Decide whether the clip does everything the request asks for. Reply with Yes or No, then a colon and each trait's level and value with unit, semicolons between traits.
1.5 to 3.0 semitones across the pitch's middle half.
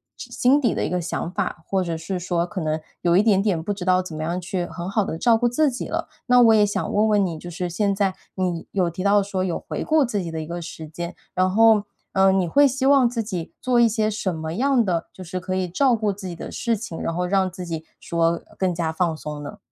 No: average, 3.9 semitones